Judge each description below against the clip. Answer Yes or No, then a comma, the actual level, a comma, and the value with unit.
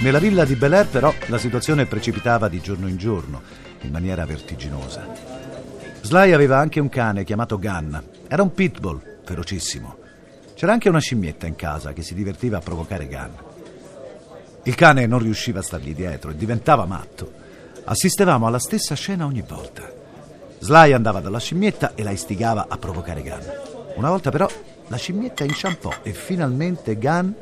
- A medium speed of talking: Yes, average, 160 wpm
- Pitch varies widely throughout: Yes, wide, 8.6 semitones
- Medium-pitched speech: No, low, 115 Hz